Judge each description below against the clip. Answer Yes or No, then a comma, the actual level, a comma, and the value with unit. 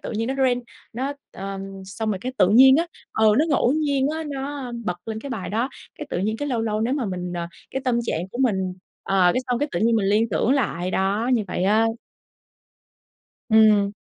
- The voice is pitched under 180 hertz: No, high, 225 Hz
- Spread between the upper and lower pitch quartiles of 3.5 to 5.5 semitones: Yes, average, 5.1 semitones